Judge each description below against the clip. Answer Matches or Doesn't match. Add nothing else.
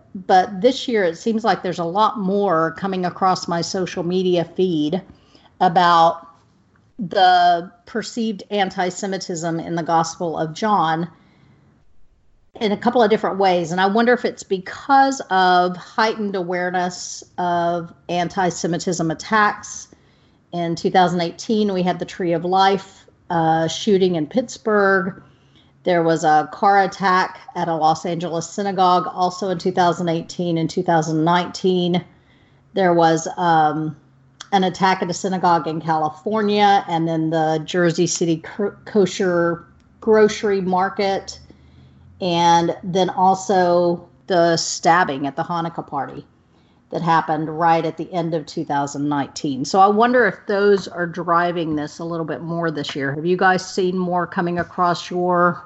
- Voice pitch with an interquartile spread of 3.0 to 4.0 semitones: Doesn't match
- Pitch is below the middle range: Doesn't match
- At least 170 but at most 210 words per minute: Doesn't match